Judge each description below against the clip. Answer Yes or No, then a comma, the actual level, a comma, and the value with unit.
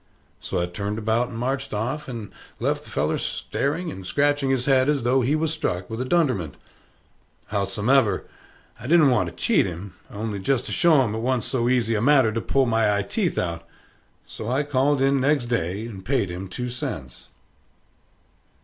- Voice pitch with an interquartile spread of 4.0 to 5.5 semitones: Yes, average, 4.9 semitones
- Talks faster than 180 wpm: Yes, average, 190 wpm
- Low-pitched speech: Yes, low, 120 Hz